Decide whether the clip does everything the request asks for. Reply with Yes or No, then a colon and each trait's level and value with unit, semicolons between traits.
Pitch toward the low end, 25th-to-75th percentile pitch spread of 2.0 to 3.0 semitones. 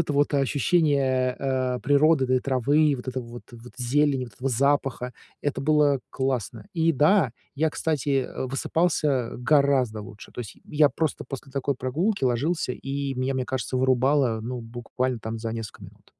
Yes: low, 130 Hz; narrow, 2.6 semitones